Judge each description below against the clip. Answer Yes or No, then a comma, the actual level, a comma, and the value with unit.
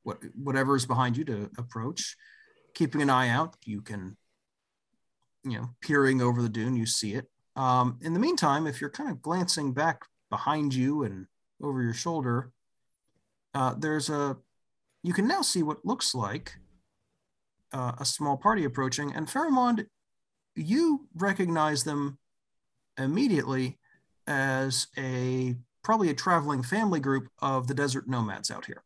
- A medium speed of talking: Yes, average, 150 wpm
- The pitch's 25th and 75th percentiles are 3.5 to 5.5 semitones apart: Yes, average, 4.4 semitones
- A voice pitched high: No, medium, 140 Hz